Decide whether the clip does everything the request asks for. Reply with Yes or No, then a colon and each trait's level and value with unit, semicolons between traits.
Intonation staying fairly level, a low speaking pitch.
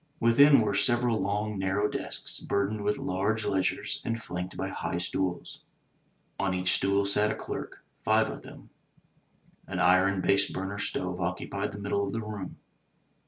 Yes: narrow, 2.1 semitones; low, 100 Hz